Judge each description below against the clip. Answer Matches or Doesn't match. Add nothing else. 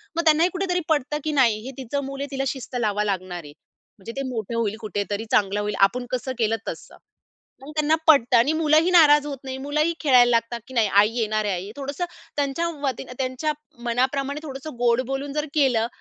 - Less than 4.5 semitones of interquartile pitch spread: Doesn't match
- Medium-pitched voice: Doesn't match